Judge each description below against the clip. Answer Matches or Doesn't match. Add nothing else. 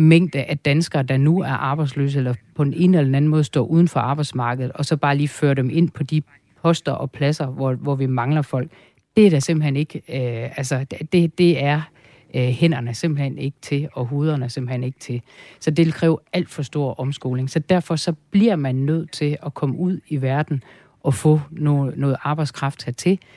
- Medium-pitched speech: Matches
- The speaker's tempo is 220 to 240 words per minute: Doesn't match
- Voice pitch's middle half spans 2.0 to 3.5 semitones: Matches